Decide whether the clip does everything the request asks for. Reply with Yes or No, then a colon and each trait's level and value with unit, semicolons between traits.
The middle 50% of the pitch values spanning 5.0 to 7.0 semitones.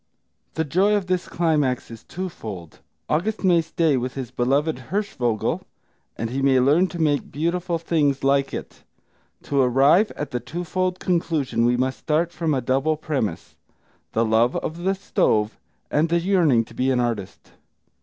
Yes: average, 5.3 semitones